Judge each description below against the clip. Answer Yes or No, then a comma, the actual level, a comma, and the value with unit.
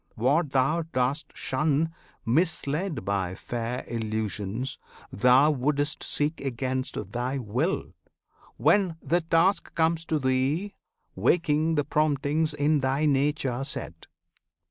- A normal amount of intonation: Yes, average, 3.8 semitones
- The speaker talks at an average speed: No, slow, 110 wpm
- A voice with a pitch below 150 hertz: Yes, medium, 140 Hz